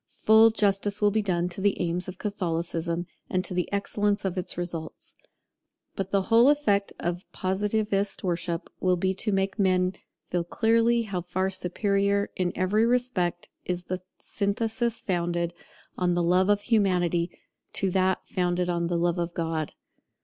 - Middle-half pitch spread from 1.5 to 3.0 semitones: Yes, narrow, 2.6 semitones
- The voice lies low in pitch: No, medium, 185 Hz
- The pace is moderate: Yes, average, 160 wpm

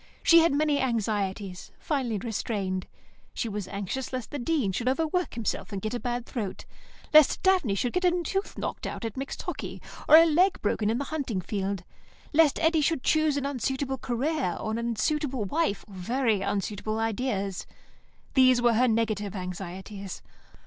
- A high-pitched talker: Yes, high, 240 Hz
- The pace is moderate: Yes, average, 170 wpm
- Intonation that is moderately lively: No, wide, 6.1 semitones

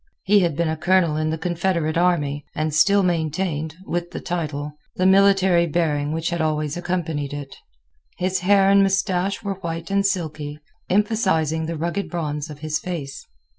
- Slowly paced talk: No, average, 170 wpm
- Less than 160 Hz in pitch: No, medium, 170 Hz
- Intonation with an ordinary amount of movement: Yes, average, 3.4 semitones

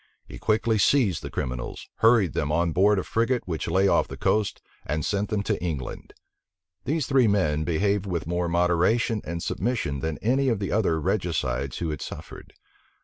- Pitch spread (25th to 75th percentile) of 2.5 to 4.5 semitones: No, average, 5.3 semitones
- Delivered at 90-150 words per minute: No, average, 180 wpm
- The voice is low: Yes, very low, 90 Hz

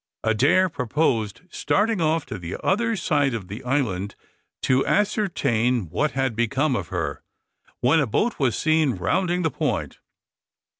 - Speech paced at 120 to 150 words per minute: Yes, average, 145 wpm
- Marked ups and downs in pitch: Yes, wide, 6.3 semitones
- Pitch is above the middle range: No, low, 135 Hz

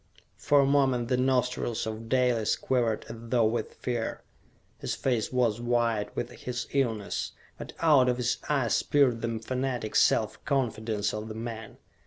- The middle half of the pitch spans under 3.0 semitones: Yes, narrow, 2.4 semitones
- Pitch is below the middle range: Yes, low, 120 Hz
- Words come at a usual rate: Yes, average, 160 wpm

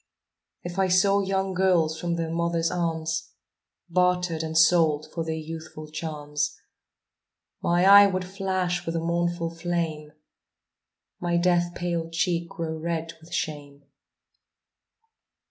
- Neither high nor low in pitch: Yes, medium, 170 Hz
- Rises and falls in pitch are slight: Yes, narrow, 1.9 semitones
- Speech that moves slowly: Yes, slow, 125 wpm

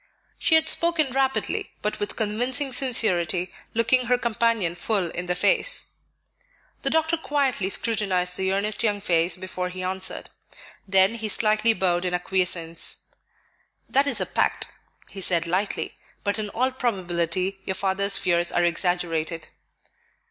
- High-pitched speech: Yes, high, 195 Hz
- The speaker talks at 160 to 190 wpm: No, average, 140 wpm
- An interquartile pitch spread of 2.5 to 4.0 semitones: No, average, 4.6 semitones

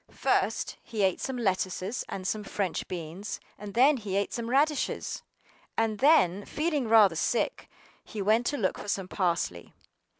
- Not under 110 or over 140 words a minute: No, average, 160 wpm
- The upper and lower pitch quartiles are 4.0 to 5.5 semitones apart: Yes, average, 4.3 semitones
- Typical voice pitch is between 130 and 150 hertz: No, high, 210 Hz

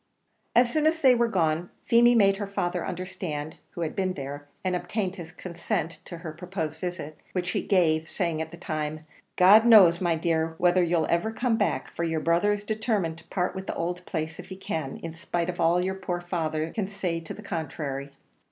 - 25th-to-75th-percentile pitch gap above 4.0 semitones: No, average, 3.1 semitones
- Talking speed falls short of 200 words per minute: No, fast, 205 wpm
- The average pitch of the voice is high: No, medium, 175 Hz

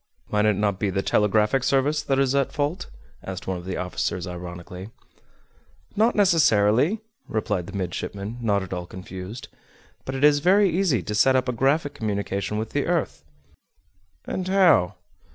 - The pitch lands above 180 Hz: No, low, 110 Hz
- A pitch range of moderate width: No, wide, 7.1 semitones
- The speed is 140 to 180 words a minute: Yes, average, 165 wpm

